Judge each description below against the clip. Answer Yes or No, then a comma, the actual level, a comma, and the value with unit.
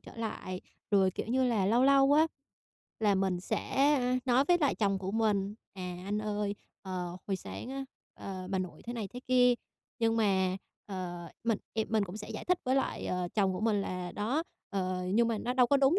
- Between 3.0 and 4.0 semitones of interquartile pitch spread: No, average, 4.6 semitones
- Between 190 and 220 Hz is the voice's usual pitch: Yes, high, 210 Hz